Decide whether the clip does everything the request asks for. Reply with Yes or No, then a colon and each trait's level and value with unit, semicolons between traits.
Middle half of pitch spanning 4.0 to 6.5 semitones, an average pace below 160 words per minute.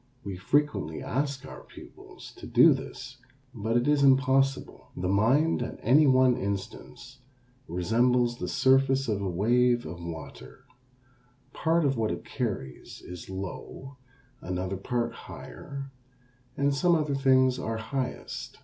Yes: average, 5.1 semitones; slow, 135 wpm